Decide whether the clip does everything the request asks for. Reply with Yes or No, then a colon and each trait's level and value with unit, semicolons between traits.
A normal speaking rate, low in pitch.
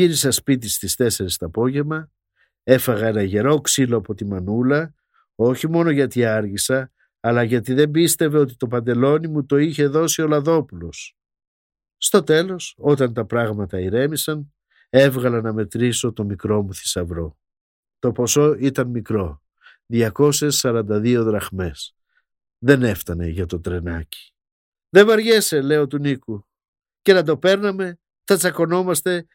Yes: average, 135 wpm; low, 125 Hz